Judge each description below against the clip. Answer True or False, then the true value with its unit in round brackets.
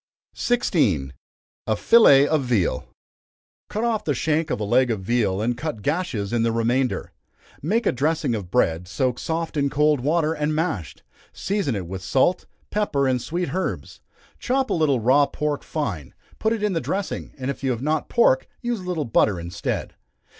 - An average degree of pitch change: False (6.2 semitones)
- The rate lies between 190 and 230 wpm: False (180 wpm)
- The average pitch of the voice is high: False (140 Hz)